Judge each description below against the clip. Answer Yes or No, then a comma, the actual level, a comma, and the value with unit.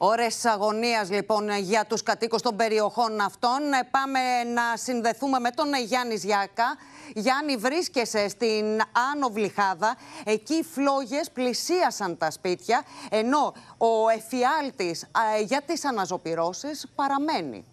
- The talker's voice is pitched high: Yes, high, 235 Hz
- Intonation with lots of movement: No, average, 4.3 semitones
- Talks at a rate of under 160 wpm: Yes, slow, 115 wpm